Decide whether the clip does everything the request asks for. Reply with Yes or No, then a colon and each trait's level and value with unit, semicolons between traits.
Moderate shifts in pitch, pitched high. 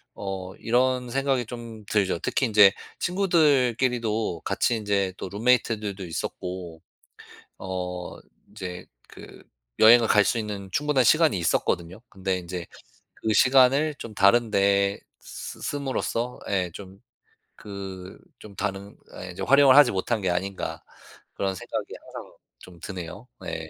No: average, 4.6 semitones; low, 100 Hz